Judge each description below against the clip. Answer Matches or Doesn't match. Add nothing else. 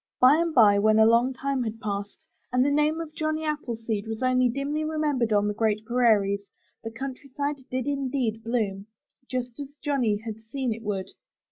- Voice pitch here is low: Doesn't match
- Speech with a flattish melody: Doesn't match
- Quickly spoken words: Doesn't match